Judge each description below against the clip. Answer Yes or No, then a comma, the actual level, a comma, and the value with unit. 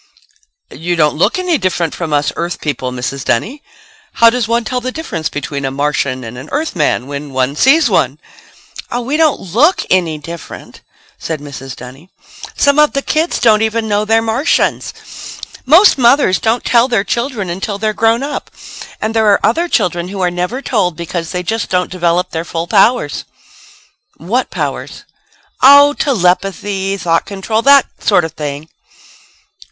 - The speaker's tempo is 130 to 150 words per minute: No, average, 165 wpm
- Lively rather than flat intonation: Yes, wide, 6.9 semitones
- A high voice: Yes, high, 195 Hz